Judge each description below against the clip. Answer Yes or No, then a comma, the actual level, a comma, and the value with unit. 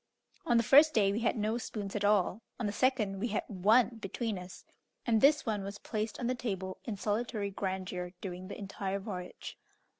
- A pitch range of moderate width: Yes, average, 3.1 semitones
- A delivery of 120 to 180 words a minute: No, average, 200 wpm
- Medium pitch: No, high, 210 Hz